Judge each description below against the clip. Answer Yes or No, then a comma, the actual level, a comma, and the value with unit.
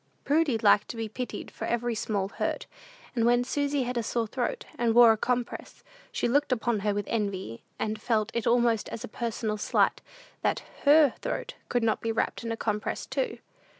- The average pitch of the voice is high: Yes, high, 230 Hz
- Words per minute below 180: No, average, 195 wpm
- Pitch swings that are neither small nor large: No, narrow, 2.1 semitones